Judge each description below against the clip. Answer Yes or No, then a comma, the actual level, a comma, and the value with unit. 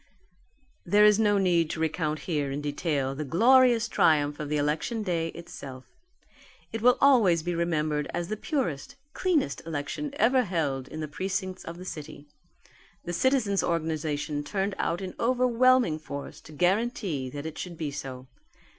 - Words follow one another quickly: No, average, 160 wpm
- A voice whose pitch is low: No, medium, 170 Hz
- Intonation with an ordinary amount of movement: No, wide, 5.9 semitones